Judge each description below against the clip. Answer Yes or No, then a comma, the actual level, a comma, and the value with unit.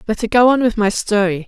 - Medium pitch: No, high, 215 Hz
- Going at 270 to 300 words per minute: Yes, fast, 285 wpm